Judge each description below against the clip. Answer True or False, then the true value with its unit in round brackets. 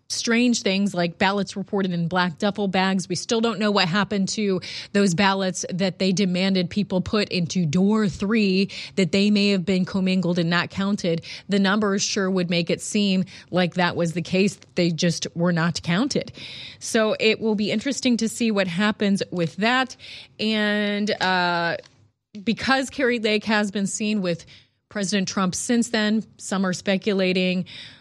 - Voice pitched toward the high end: True (195 Hz)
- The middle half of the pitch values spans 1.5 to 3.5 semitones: True (2.8 semitones)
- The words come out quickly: False (170 wpm)